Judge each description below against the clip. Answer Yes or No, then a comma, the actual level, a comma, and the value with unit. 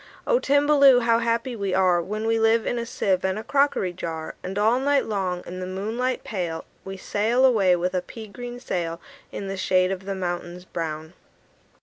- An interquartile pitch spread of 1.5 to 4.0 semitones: No, average, 4.4 semitones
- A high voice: Yes, high, 195 Hz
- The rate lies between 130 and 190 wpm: No, average, 200 wpm